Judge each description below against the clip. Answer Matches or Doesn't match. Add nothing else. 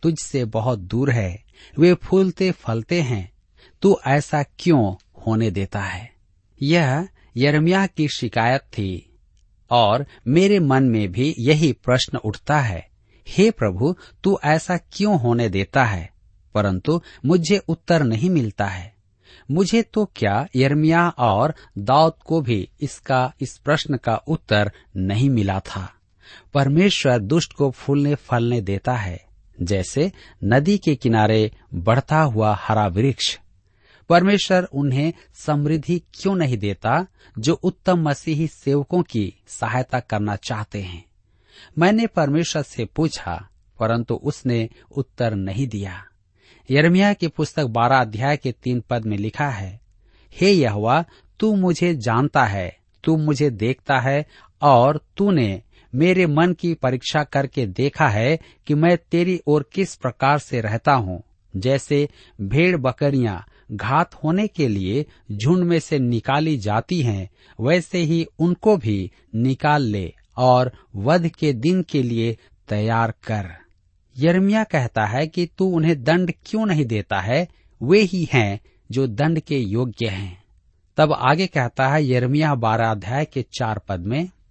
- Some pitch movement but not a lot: Doesn't match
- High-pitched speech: Doesn't match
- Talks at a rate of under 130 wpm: Doesn't match